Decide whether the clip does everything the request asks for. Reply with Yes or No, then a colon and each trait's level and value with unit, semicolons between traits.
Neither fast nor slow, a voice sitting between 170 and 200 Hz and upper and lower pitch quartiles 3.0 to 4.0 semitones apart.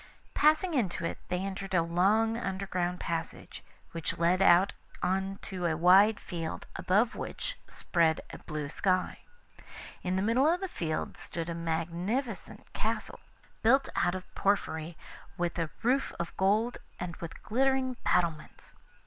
No: average, 145 wpm; medium, 185 Hz; average, 4.6 semitones